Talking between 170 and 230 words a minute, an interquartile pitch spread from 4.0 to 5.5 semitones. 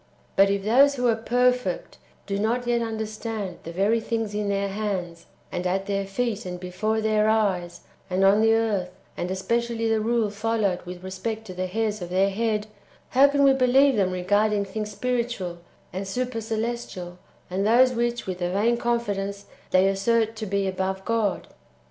No: average, 180 wpm; average, 3.2 semitones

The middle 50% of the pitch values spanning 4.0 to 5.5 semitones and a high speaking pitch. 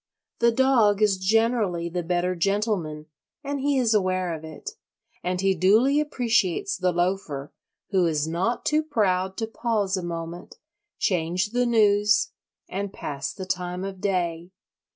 Yes: average, 4.3 semitones; high, 195 Hz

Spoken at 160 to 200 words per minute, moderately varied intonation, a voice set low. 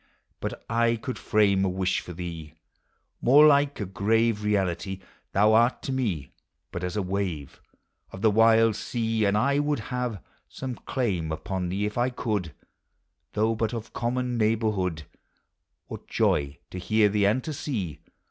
Yes: average, 165 wpm; average, 4.0 semitones; low, 105 Hz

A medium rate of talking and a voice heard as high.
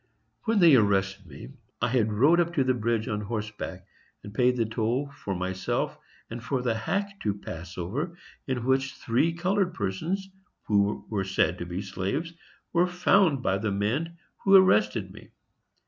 No: average, 170 wpm; low, 115 Hz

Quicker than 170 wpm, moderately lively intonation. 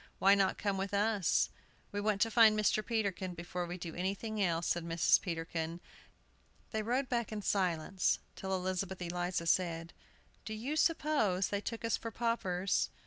No: average, 165 wpm; average, 3.6 semitones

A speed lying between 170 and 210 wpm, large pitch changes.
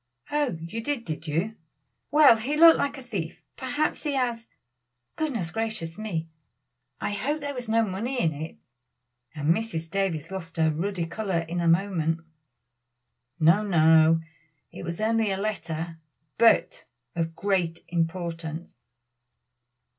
No: average, 140 wpm; wide, 5.7 semitones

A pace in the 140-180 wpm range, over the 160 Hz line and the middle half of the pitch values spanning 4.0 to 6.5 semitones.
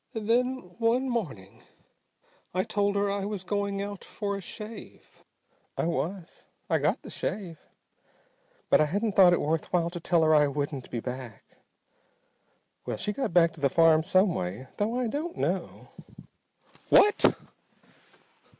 Yes: average, 155 wpm; medium, 185 Hz; average, 4.9 semitones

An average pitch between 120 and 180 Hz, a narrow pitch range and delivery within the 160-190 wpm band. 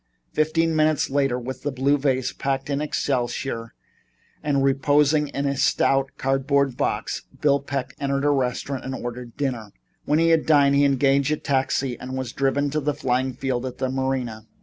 Yes: low, 135 Hz; narrow, 1.7 semitones; average, 175 wpm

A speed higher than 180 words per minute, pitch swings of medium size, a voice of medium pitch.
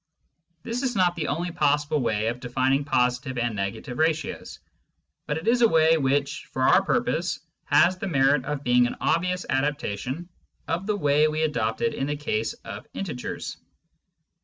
No: average, 165 wpm; average, 4.5 semitones; medium, 145 Hz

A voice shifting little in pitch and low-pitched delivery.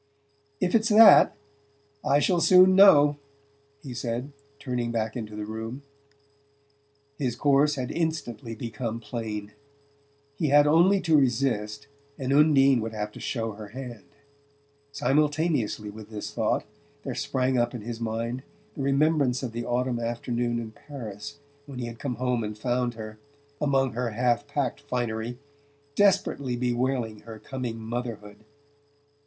No: average, 3.9 semitones; low, 125 Hz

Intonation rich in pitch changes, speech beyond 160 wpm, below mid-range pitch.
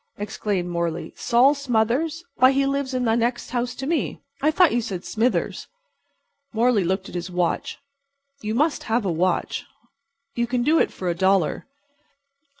No: wide, 5.7 semitones; average, 170 wpm; high, 235 Hz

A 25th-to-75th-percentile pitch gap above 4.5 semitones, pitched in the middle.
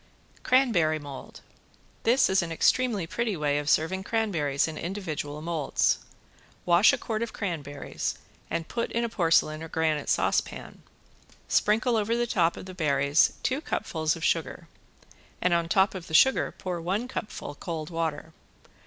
Yes: average, 5.3 semitones; medium, 170 Hz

